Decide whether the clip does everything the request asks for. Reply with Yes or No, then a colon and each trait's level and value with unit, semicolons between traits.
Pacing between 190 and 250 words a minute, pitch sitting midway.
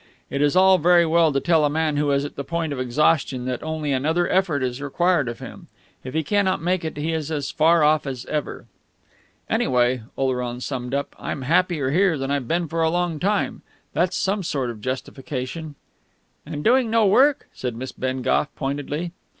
Yes: average, 200 wpm; medium, 150 Hz